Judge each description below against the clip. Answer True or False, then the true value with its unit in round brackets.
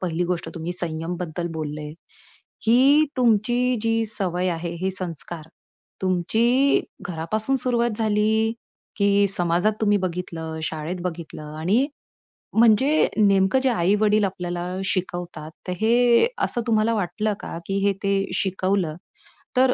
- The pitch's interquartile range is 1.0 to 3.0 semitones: False (4.4 semitones)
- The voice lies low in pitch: False (195 Hz)